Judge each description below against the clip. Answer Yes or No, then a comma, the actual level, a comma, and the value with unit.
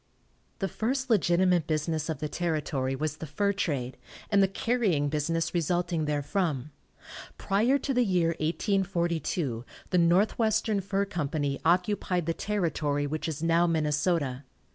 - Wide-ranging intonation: No, average, 4.5 semitones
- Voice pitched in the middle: Yes, medium, 170 Hz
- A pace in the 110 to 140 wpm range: Yes, slow, 135 wpm